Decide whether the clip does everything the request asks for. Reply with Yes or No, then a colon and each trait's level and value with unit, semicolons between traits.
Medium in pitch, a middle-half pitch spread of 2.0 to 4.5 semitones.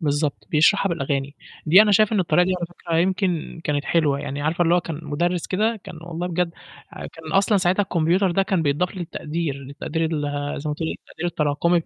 Yes: medium, 165 Hz; average, 3.3 semitones